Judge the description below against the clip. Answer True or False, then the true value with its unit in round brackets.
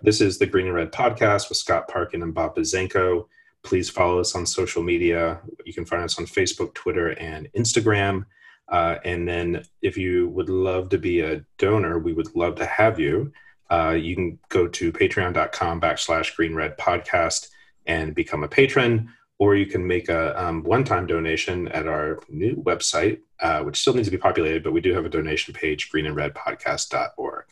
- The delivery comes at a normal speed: True (180 wpm)